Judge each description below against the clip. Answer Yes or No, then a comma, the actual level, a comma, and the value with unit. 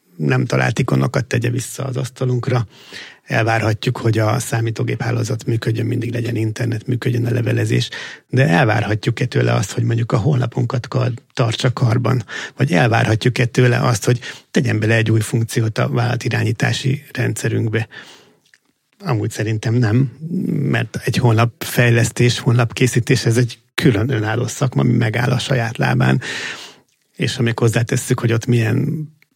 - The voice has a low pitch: Yes, low, 120 Hz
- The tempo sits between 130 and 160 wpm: Yes, average, 135 wpm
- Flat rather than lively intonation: Yes, narrow, 2.1 semitones